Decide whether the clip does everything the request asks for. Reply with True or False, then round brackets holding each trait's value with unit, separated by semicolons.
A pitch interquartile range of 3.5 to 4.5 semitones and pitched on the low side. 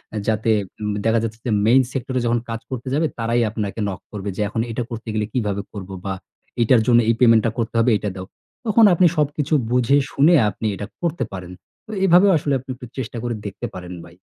True (3.9 semitones; 115 Hz)